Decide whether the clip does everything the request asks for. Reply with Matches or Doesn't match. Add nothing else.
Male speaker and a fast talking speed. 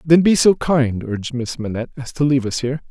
Matches